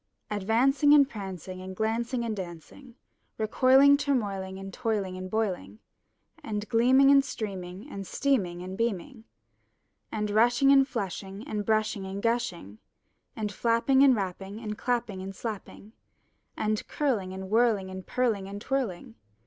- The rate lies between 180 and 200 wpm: No, average, 140 wpm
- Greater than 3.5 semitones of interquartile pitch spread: Yes, average, 4.2 semitones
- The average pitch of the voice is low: No, high, 215 Hz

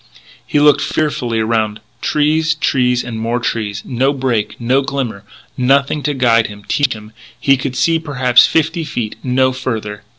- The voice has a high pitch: No, low, 125 Hz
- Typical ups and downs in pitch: Yes, average, 3.6 semitones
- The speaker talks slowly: No, average, 160 wpm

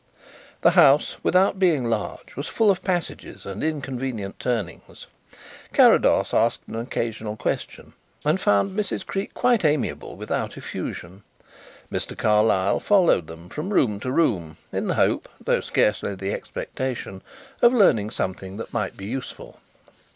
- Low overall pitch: Yes, low, 120 Hz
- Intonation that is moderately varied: No, wide, 8.6 semitones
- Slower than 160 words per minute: Yes, average, 140 wpm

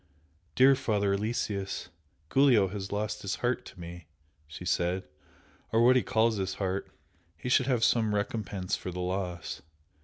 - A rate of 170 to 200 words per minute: No, average, 155 wpm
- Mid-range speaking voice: No, low, 100 Hz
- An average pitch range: Yes, average, 3.8 semitones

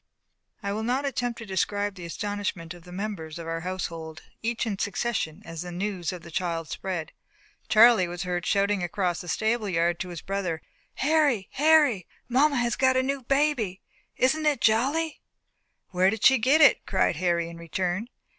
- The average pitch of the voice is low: No, high, 200 Hz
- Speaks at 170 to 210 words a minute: Yes, average, 180 wpm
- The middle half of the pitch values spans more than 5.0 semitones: Yes, wide, 5.6 semitones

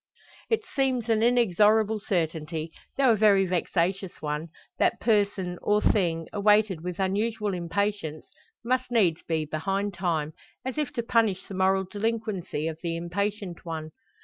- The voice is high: Yes, high, 195 Hz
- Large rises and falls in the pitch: No, average, 4.4 semitones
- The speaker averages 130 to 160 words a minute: Yes, average, 145 wpm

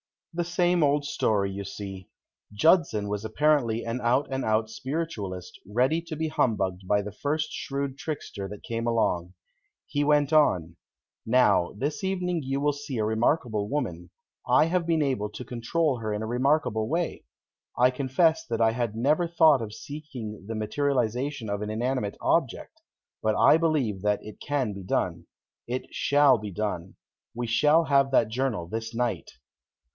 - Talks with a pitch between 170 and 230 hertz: No, low, 125 Hz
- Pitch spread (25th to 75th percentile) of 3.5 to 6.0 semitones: Yes, wide, 5.6 semitones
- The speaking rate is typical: Yes, average, 165 wpm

